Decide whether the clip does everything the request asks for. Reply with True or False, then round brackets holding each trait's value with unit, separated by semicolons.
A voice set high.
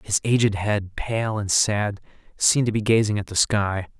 False (105 Hz)